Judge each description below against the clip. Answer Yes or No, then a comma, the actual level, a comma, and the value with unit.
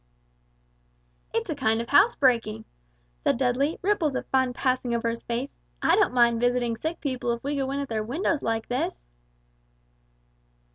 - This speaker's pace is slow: No, average, 160 wpm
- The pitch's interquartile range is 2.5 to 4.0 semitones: Yes, average, 3.2 semitones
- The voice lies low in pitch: No, very high, 250 Hz